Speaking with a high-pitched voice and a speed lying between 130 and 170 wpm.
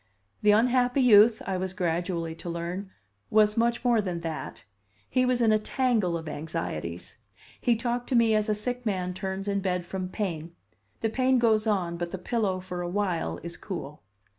No: high, 195 Hz; average, 190 wpm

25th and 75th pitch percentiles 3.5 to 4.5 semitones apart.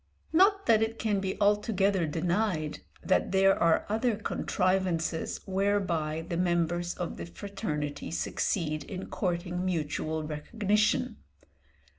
Yes: average, 4.0 semitones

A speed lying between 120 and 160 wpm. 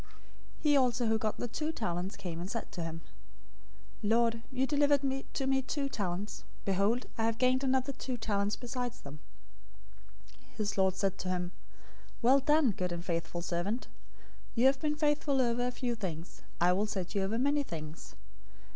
No: average, 175 wpm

